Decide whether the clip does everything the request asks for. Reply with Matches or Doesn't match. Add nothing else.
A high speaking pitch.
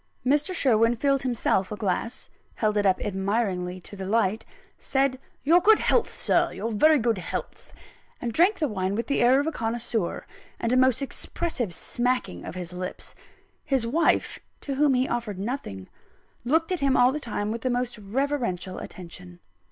Matches